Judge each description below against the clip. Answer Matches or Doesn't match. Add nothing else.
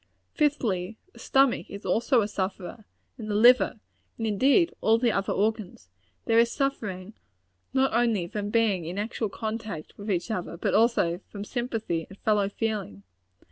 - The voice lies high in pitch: Matches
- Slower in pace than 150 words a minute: Doesn't match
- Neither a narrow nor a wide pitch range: Matches